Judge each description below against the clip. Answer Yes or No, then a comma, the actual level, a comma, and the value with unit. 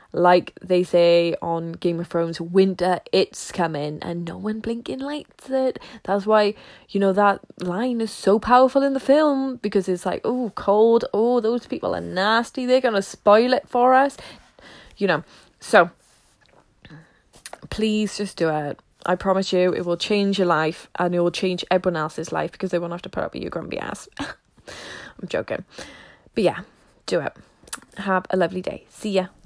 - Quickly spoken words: No, average, 185 wpm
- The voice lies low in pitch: No, high, 195 Hz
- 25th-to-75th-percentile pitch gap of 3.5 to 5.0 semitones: Yes, average, 4.5 semitones